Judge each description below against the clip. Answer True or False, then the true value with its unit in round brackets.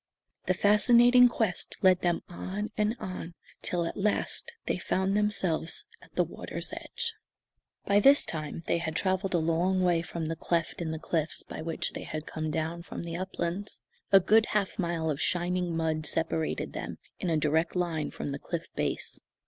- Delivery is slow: False (180 wpm)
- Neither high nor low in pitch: True (175 Hz)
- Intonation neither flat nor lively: True (3.0 semitones)